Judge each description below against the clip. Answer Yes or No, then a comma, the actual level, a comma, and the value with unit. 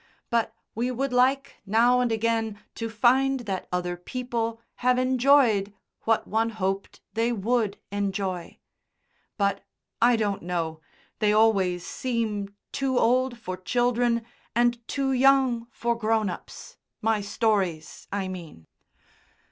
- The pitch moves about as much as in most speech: Yes, average, 3.6 semitones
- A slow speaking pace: Yes, slow, 125 wpm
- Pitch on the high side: Yes, high, 225 Hz